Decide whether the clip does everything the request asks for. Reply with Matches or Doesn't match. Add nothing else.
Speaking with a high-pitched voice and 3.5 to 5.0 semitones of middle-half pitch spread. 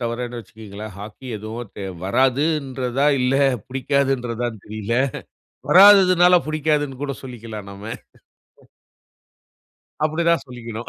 Doesn't match